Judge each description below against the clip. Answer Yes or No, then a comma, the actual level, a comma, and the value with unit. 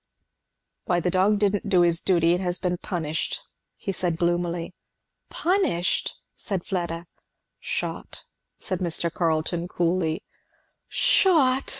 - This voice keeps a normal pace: No, slow, 115 wpm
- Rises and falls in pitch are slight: Yes, narrow, 2.1 semitones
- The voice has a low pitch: No, medium, 175 Hz